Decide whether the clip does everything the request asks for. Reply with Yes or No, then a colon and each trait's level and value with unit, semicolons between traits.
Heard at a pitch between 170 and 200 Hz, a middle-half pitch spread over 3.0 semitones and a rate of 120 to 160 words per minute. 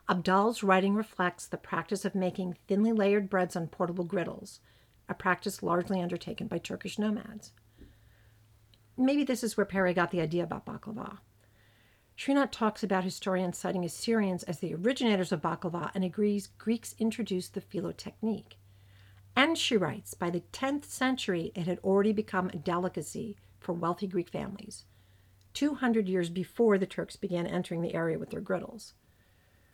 Yes: medium, 185 Hz; average, 3.8 semitones; average, 155 wpm